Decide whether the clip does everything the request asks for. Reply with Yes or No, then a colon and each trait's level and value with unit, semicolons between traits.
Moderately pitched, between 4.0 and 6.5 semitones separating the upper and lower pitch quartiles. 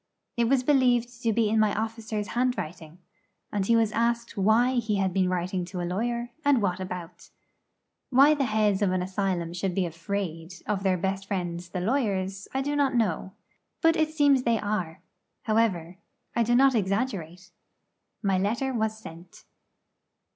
No: high, 210 Hz; average, 4.4 semitones